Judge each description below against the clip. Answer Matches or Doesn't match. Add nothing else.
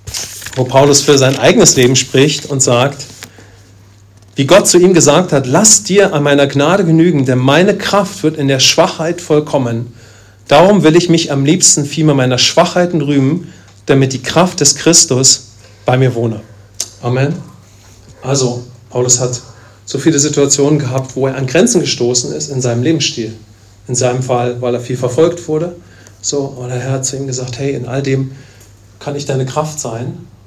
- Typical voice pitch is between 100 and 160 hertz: Matches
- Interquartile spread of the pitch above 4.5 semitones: Doesn't match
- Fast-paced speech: Doesn't match